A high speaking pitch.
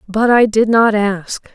Yes: high, 215 Hz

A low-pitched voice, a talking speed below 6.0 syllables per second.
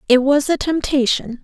No: very high, 270 Hz; 4.8 syllables/s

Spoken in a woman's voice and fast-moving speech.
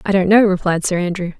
Yes: female; fast, 260 wpm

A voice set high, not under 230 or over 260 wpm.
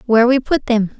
Yes: high, 240 Hz; fast, 240 wpm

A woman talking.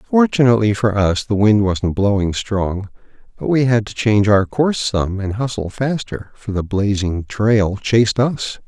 No: male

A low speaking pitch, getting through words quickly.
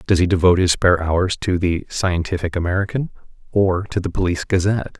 No: very low, 90 Hz; average, 180 wpm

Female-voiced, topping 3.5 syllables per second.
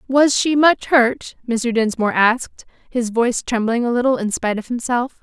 Yes: female; 5.1 syllables/s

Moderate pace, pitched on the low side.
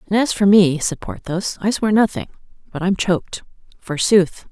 No: average, 175 wpm; high, 190 Hz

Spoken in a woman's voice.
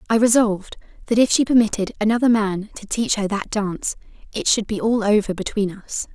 Yes: female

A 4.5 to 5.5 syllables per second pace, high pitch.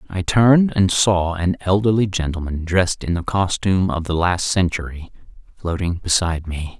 No: 5.1 syllables/s; very low, 90 Hz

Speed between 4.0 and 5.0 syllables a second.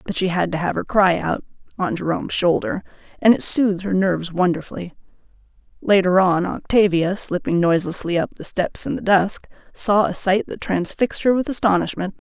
No: 5.5 syllables/s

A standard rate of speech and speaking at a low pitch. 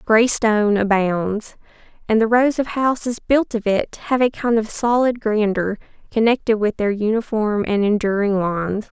No: average, 160 wpm; high, 220 Hz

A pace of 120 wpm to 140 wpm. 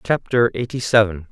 Yes: slow, 135 wpm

